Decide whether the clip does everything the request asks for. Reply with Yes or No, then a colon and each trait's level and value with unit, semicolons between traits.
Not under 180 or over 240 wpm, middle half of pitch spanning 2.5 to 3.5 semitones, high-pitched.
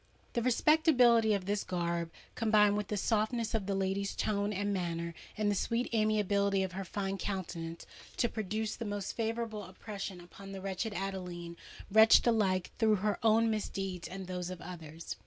No: average, 165 wpm; average, 2.8 semitones; high, 200 Hz